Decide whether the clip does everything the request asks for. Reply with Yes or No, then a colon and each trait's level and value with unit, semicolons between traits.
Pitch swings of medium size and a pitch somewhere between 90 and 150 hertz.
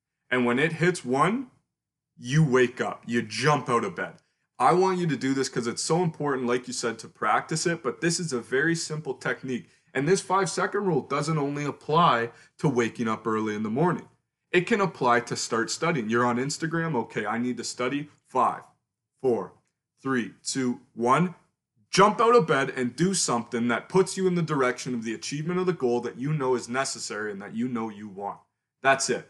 No: wide, 5.7 semitones; low, 135 Hz